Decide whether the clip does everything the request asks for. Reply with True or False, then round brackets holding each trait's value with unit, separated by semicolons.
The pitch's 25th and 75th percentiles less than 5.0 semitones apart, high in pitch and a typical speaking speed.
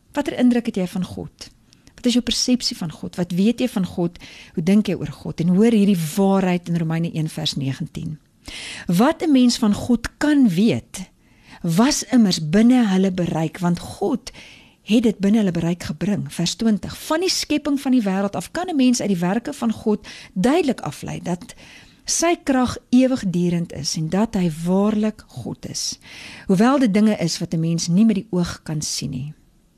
False (5.6 semitones; 195 Hz; 185 wpm)